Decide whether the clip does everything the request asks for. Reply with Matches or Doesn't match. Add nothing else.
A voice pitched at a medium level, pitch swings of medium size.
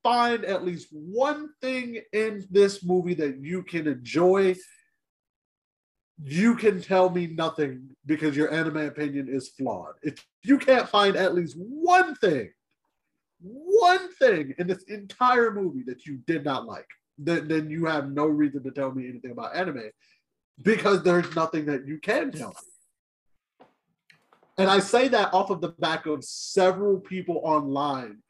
Doesn't match